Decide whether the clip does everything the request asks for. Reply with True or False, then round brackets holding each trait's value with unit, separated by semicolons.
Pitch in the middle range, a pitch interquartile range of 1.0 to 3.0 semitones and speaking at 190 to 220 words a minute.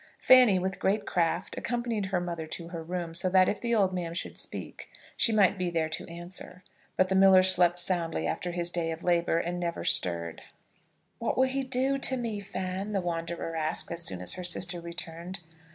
True (180 Hz; 2.4 semitones; 200 wpm)